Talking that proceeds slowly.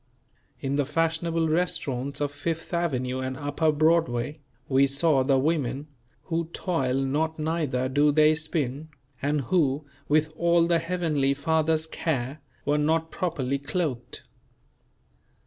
Yes: slow, 130 wpm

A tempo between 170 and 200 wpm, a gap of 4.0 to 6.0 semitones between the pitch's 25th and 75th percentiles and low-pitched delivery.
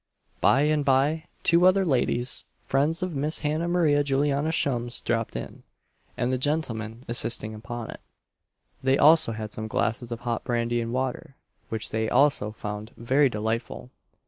No: average, 155 wpm; average, 4.3 semitones; low, 125 Hz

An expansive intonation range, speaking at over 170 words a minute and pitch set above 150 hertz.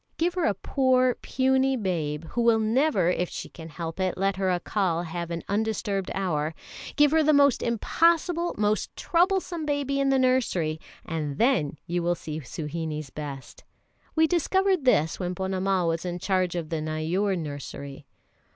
No: wide, 8.3 semitones; average, 165 wpm; high, 190 Hz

